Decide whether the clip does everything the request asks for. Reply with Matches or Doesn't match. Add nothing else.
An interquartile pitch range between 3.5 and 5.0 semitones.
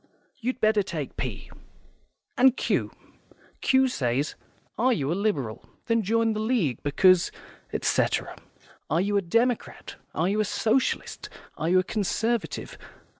Doesn't match